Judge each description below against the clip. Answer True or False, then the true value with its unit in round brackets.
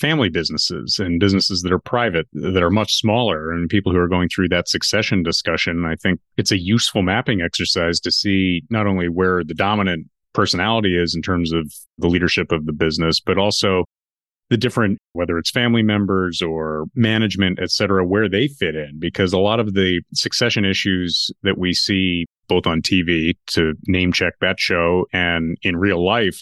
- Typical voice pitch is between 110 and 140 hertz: False (90 Hz)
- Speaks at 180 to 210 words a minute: True (185 wpm)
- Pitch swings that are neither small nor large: True (3.1 semitones)